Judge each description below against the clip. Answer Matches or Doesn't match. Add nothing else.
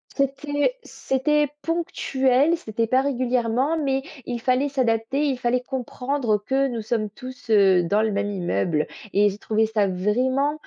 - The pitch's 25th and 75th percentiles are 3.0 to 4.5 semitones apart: Matches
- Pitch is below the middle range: Doesn't match